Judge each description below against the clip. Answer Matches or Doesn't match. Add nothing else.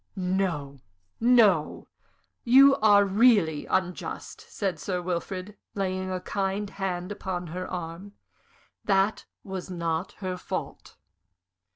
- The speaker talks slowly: Matches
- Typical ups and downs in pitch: Doesn't match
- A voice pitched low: Doesn't match